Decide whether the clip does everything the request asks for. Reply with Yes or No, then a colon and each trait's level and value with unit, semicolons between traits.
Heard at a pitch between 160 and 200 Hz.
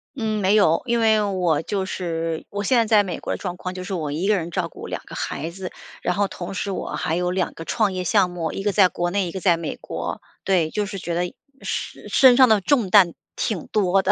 Yes: medium, 185 Hz